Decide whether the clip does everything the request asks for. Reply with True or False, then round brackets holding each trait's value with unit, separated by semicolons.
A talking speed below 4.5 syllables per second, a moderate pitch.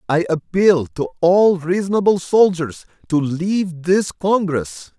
True (3.9 syllables/s; 170 Hz)